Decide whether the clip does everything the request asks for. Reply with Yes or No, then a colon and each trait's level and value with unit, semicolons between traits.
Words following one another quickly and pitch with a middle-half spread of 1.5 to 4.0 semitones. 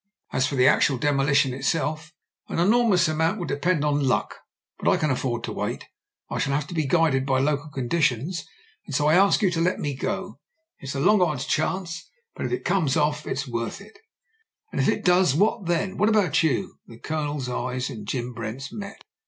No: fast, 210 wpm; average, 4.6 semitones